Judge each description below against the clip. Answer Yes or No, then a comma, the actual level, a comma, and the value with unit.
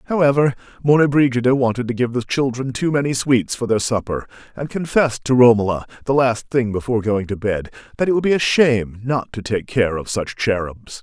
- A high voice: No, low, 120 Hz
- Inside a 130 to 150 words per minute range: No, fast, 205 wpm